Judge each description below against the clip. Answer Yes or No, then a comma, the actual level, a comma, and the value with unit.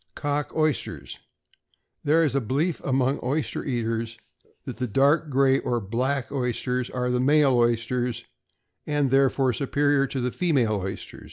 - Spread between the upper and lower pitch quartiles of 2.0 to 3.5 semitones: Yes, average, 2.8 semitones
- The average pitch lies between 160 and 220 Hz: No, low, 130 Hz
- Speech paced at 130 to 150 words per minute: Yes, average, 145 wpm